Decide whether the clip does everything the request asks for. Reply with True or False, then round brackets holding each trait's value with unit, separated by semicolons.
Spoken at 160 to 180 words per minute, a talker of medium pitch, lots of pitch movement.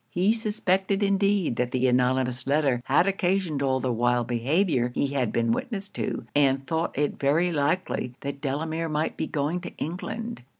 True (170 wpm; 145 Hz; 6.0 semitones)